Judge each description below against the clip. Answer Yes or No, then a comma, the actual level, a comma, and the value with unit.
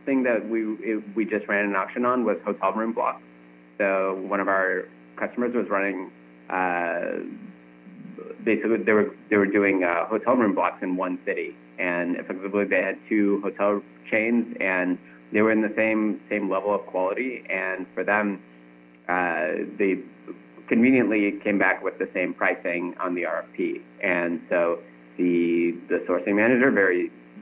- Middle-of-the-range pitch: No, very low, 95 Hz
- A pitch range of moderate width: Yes, average, 3.5 semitones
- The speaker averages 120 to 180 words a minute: Yes, average, 160 wpm